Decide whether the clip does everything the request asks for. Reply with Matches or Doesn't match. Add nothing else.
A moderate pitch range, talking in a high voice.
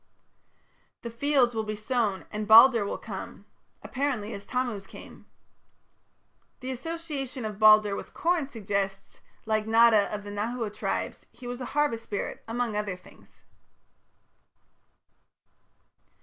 Matches